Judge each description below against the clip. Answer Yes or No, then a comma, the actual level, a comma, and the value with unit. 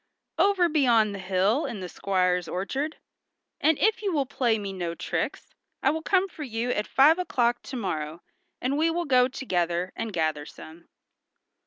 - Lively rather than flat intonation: Yes, wide, 8.3 semitones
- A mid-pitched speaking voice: No, high, 235 Hz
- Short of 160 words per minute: No, average, 175 wpm